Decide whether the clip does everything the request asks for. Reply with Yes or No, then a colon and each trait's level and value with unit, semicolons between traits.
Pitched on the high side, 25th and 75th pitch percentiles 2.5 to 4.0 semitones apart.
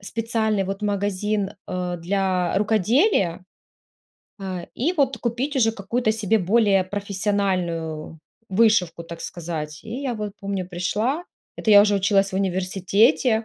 Yes: high, 200 Hz; average, 3.3 semitones